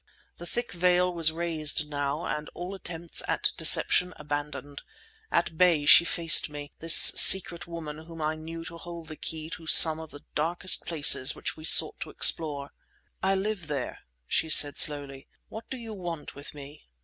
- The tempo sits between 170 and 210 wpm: Yes, average, 175 wpm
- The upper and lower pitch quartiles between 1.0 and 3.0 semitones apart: Yes, narrow, 2.6 semitones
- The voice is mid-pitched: Yes, medium, 160 Hz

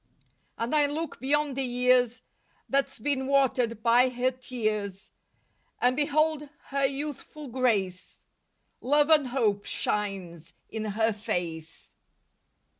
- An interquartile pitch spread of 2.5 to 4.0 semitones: No, average, 4.5 semitones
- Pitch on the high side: Yes, very high, 250 Hz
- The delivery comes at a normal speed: No, slow, 115 wpm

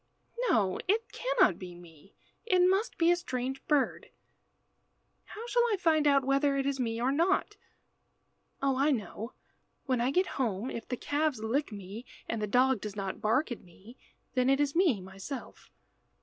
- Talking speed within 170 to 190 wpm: Yes, average, 175 wpm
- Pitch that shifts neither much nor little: No, wide, 5.8 semitones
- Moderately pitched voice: No, very high, 265 Hz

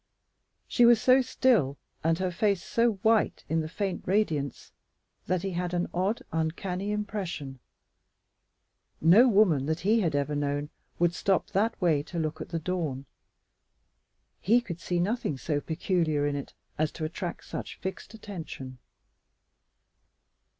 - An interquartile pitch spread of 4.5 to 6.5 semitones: Yes, average, 4.8 semitones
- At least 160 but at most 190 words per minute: No, average, 145 wpm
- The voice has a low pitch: No, medium, 175 Hz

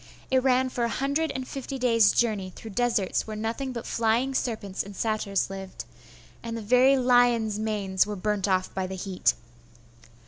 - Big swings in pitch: No, average, 3.8 semitones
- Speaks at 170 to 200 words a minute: Yes, average, 175 wpm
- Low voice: No, high, 225 Hz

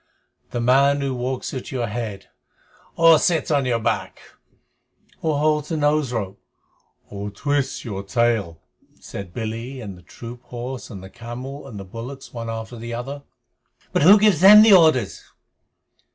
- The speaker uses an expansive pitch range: No, average, 4.1 semitones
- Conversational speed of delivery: Yes, average, 160 wpm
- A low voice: Yes, low, 125 Hz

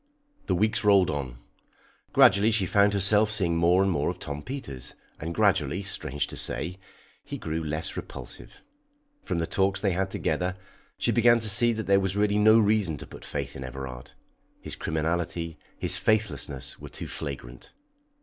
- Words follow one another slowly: No, average, 170 wpm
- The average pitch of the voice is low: Yes, very low, 95 Hz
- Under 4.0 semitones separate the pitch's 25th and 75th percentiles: No, average, 5.0 semitones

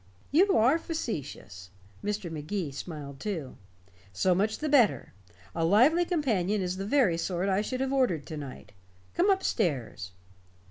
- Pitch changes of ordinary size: No, wide, 8.9 semitones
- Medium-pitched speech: No, high, 195 Hz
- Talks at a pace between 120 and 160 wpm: Yes, average, 150 wpm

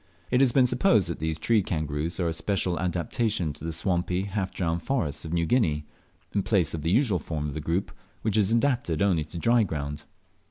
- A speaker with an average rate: No, fast, 210 wpm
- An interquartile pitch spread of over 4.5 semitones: Yes, average, 5.0 semitones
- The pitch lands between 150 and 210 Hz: No, very low, 90 Hz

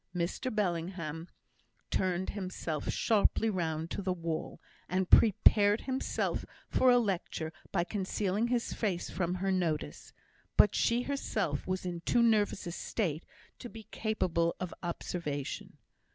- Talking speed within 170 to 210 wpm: No, slow, 135 wpm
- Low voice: No, medium, 185 Hz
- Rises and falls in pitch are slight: No, average, 4.1 semitones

